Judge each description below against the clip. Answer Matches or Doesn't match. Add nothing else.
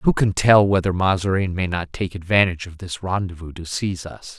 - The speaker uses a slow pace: Doesn't match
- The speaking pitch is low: Matches